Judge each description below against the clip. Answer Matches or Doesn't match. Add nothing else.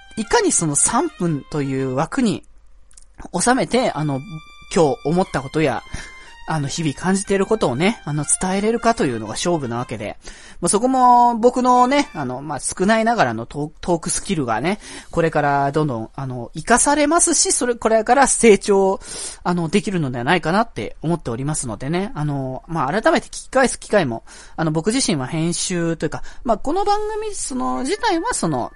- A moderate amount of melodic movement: Doesn't match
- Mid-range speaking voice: Matches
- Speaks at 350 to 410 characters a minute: Matches